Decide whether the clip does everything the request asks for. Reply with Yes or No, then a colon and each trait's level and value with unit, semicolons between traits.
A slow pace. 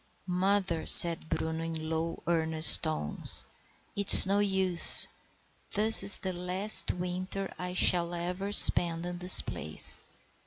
Yes: slow, 125 wpm